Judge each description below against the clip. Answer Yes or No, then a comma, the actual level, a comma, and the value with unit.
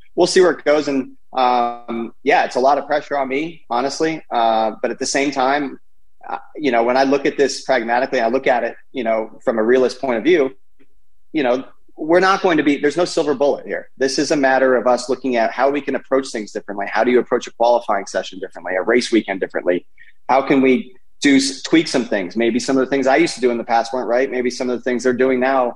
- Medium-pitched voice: No, low, 130 Hz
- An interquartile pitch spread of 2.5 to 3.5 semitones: Yes, average, 2.9 semitones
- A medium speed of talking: No, fast, 255 wpm